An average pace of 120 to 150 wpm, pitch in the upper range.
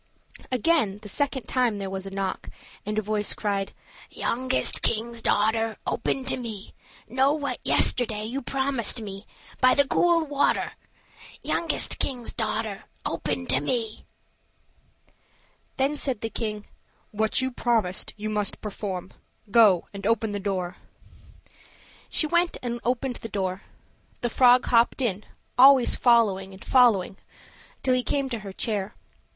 Yes: average, 145 wpm; high, 225 Hz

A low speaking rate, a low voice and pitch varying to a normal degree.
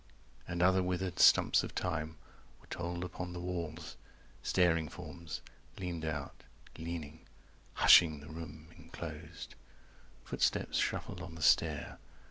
No: slow, 120 wpm; very low, 85 Hz; narrow, 2.0 semitones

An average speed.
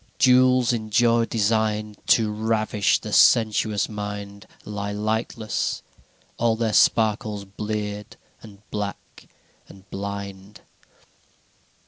No: slow, 100 wpm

